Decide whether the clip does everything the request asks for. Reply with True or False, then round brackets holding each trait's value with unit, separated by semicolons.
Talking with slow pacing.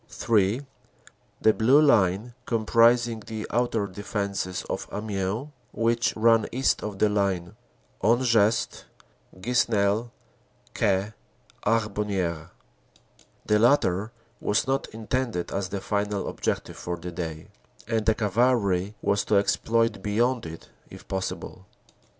True (115 wpm)